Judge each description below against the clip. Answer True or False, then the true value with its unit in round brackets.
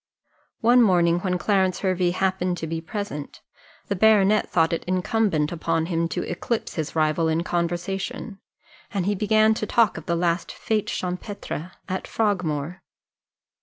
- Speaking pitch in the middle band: True (180 Hz)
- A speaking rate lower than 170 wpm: True (150 wpm)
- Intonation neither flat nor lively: True (3.4 semitones)